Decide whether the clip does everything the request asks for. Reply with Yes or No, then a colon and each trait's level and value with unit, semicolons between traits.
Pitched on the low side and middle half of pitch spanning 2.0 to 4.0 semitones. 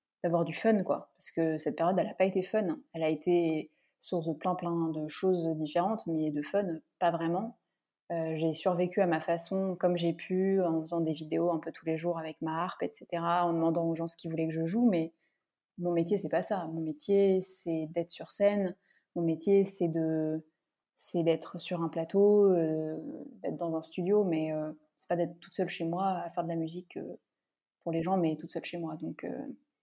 No: medium, 170 Hz; narrow, 2.4 semitones